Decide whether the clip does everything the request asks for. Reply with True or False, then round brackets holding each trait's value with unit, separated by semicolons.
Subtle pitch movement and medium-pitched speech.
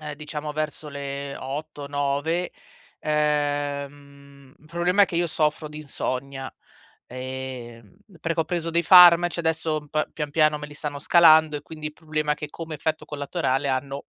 True (2.0 semitones; 150 Hz)